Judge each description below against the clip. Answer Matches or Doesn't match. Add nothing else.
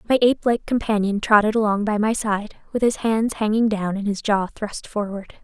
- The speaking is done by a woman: Matches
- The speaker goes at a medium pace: Doesn't match